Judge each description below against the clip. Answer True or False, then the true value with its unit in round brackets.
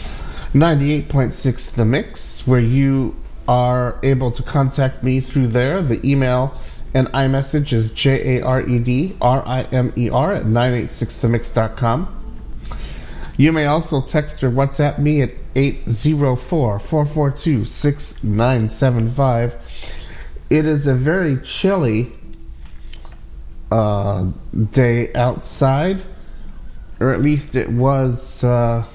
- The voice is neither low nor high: False (130 Hz)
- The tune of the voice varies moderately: True (3.0 semitones)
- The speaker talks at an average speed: False (115 wpm)